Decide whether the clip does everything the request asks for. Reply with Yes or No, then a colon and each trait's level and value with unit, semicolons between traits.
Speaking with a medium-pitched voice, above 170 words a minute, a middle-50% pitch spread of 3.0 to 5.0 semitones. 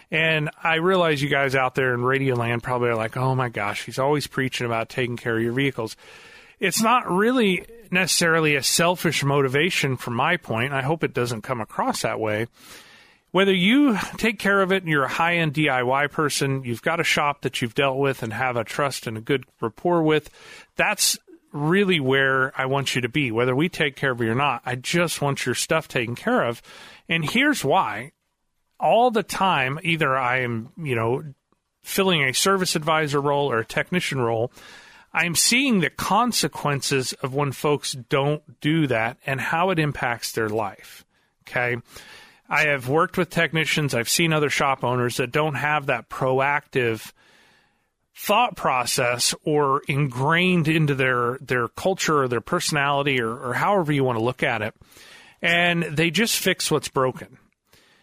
Yes: medium, 145 Hz; average, 180 wpm; average, 4.6 semitones